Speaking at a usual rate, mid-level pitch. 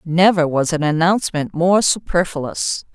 No: slow, 120 wpm; medium, 170 Hz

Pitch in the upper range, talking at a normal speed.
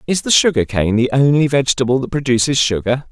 No: low, 130 Hz; average, 195 wpm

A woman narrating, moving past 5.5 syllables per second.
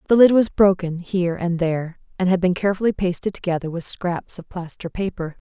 Yes: female; 5.8 syllables/s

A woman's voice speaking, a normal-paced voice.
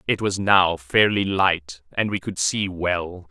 No: male; average, 180 wpm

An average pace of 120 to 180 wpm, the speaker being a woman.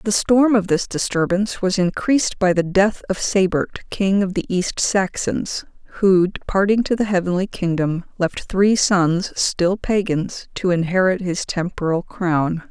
Yes: average, 155 wpm; female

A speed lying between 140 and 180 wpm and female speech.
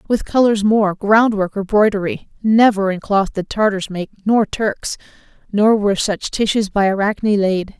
Yes: average, 160 wpm; female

